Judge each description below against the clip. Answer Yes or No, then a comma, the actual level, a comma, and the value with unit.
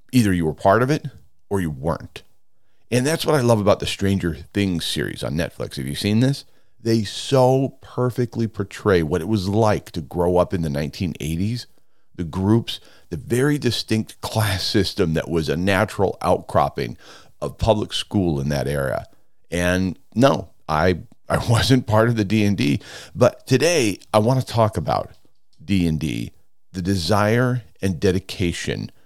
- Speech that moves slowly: No, average, 160 wpm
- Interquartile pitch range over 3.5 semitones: Yes, average, 4.7 semitones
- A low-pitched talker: Yes, low, 100 Hz